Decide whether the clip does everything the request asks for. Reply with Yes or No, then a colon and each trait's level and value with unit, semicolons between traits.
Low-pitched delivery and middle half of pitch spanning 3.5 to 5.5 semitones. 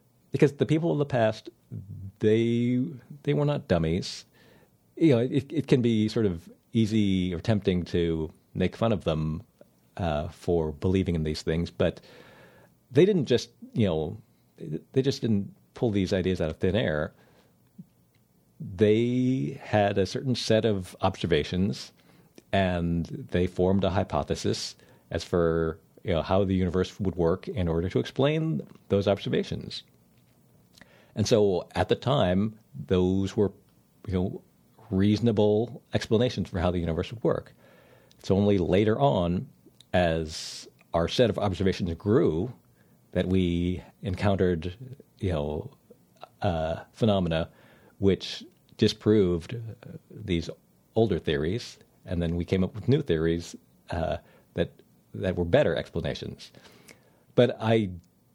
Yes: low, 100 Hz; average, 4.5 semitones